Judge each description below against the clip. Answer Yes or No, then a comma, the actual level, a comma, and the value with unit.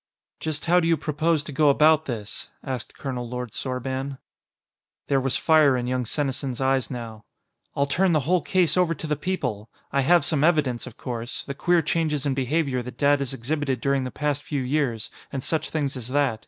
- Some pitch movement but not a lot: Yes, average, 3.4 semitones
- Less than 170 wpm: No, average, 200 wpm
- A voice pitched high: No, medium, 140 Hz